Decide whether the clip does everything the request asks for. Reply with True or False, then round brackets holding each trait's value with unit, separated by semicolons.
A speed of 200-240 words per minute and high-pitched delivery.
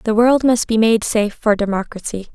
True (205 wpm; 220 Hz)